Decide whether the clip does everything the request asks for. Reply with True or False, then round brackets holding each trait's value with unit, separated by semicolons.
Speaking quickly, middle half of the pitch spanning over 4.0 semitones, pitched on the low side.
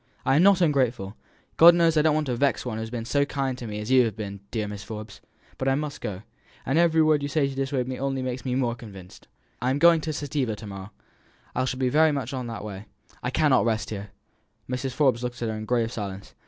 True (255 wpm; 4.4 semitones; 125 Hz)